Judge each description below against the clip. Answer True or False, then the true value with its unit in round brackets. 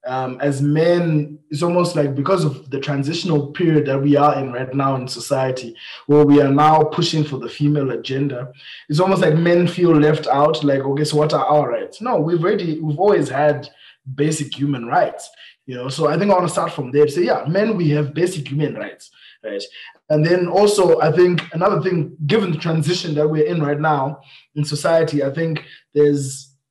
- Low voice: False (150 Hz)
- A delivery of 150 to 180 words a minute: False (205 wpm)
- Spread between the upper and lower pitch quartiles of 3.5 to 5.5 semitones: False (3.1 semitones)